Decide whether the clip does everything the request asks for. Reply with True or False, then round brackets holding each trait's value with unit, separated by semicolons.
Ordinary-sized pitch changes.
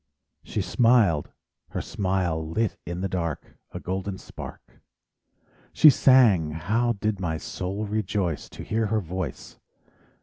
True (4.1 semitones)